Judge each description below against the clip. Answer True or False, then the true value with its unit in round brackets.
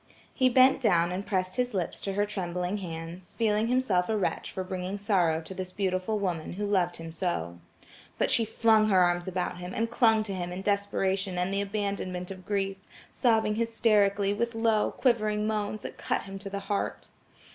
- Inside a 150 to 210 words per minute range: True (190 wpm)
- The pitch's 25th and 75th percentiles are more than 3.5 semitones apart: False (2.9 semitones)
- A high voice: True (200 Hz)